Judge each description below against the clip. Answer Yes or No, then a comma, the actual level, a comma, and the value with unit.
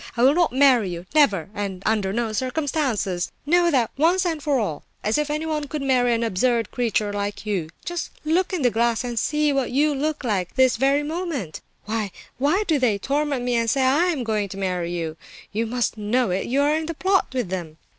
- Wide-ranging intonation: Yes, wide, 6.2 semitones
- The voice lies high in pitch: Yes, very high, 250 Hz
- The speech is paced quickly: Yes, fast, 215 wpm